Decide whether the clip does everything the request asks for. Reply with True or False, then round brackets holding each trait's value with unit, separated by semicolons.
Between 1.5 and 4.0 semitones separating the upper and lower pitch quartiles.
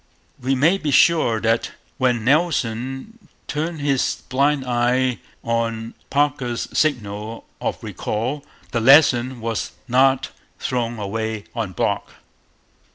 True (3.6 semitones)